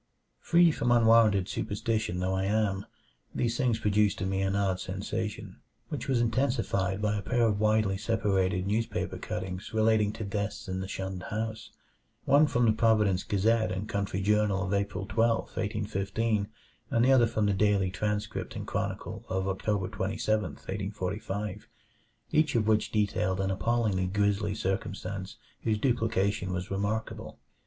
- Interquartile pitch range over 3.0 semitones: No, narrow, 2.5 semitones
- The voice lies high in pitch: No, low, 105 Hz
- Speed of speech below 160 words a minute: Yes, average, 150 wpm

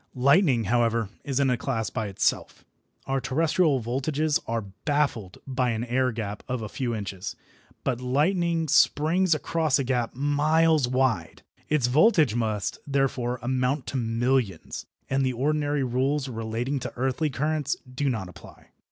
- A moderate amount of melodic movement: Yes, average, 3.7 semitones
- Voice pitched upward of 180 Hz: No, low, 130 Hz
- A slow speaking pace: No, average, 150 wpm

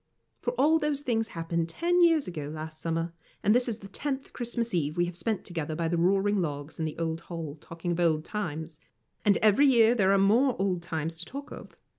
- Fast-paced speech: Yes, fast, 220 wpm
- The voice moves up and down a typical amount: No, wide, 6.2 semitones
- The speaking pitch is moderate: Yes, medium, 180 Hz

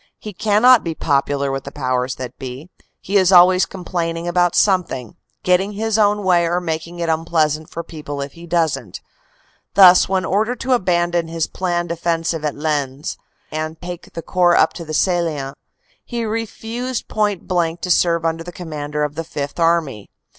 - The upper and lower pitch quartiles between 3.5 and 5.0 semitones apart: No, average, 3.1 semitones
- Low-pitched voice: No, medium, 170 Hz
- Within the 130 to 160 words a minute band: No, average, 175 wpm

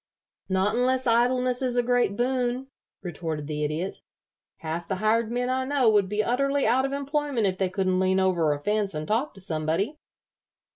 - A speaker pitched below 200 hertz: No, high, 215 Hz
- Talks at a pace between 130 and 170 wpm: No, average, 185 wpm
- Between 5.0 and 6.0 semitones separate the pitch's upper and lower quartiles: Yes, average, 5.3 semitones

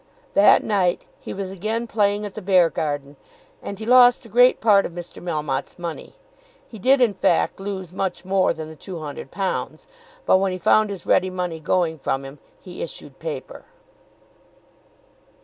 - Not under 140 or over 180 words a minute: Yes, average, 165 wpm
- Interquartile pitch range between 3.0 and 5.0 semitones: Yes, average, 4.1 semitones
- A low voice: No, medium, 185 Hz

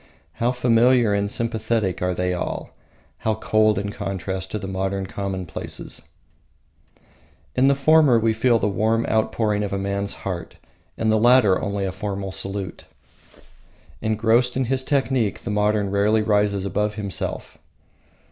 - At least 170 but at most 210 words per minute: No, average, 140 wpm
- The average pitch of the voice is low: Yes, low, 105 Hz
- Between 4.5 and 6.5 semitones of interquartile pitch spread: No, average, 2.7 semitones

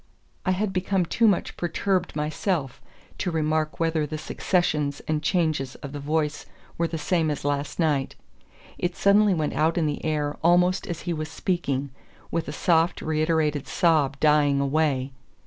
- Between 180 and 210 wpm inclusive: No, average, 165 wpm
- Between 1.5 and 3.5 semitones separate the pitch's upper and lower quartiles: Yes, average, 2.8 semitones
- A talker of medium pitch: Yes, medium, 155 Hz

